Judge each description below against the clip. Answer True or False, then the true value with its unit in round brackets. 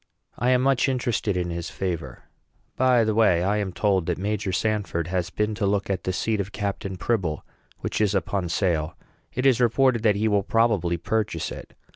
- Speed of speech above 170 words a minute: True (195 wpm)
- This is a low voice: True (100 Hz)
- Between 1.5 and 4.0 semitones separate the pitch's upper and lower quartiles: True (3.7 semitones)